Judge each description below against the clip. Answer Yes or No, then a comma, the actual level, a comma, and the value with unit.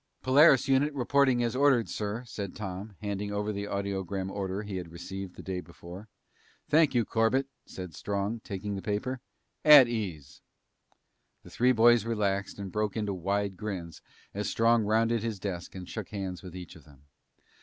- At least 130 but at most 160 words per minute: No, average, 170 wpm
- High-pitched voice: No, low, 105 Hz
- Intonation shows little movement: No, average, 3.4 semitones